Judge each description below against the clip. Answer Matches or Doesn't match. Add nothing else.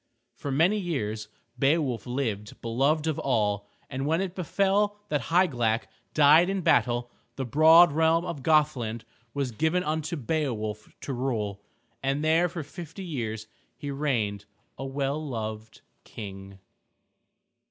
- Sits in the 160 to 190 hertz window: Doesn't match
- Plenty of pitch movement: Matches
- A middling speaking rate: Doesn't match